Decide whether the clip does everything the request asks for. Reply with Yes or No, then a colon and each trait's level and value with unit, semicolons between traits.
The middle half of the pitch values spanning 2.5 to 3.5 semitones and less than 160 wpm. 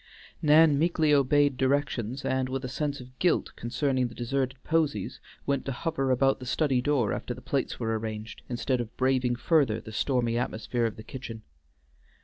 No: average, 2.9 semitones; average, 175 wpm